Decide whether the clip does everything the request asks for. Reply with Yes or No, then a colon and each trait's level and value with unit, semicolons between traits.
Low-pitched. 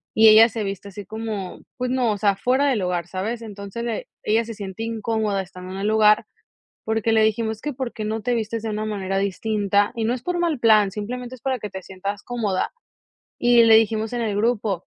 No: high, 220 Hz